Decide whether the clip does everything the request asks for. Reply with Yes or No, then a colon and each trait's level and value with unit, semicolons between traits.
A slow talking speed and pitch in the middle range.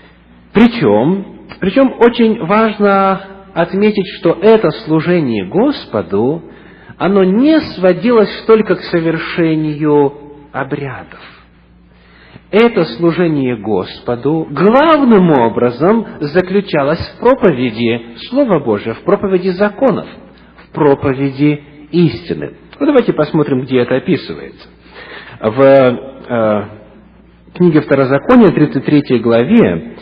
Yes: slow, 90 wpm; medium, 160 Hz